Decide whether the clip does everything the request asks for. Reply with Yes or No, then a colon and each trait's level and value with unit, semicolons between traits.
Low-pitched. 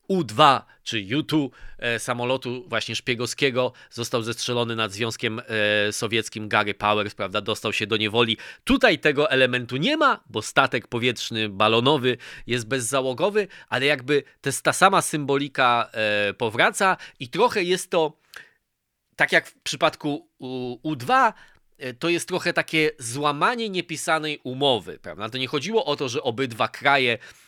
Yes: low, 125 Hz